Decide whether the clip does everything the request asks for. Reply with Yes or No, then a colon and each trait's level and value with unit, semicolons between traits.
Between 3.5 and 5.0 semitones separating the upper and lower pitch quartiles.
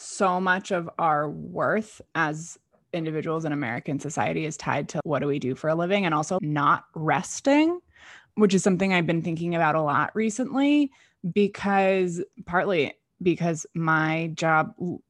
Yes: average, 3.8 semitones